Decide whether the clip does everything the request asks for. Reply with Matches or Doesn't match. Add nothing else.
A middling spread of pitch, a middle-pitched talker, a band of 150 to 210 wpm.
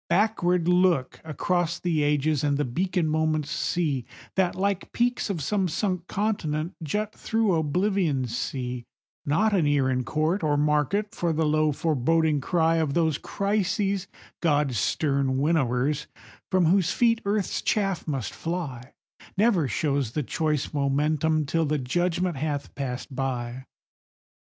Doesn't match